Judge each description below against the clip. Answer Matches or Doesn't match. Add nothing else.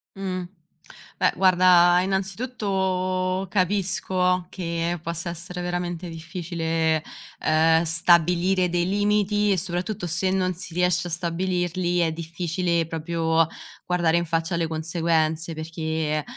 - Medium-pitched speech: Matches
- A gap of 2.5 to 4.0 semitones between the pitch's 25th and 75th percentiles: Doesn't match